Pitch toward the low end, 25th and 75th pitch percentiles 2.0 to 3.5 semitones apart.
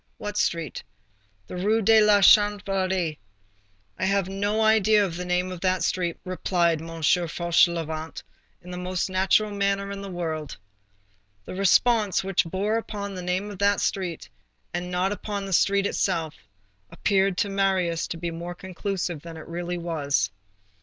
No: medium, 185 Hz; narrow, 2.6 semitones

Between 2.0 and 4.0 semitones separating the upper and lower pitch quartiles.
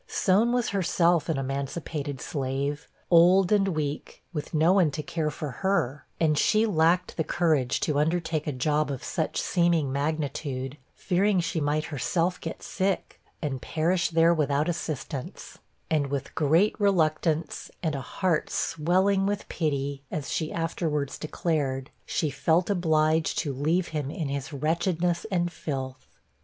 Yes: average, 3.3 semitones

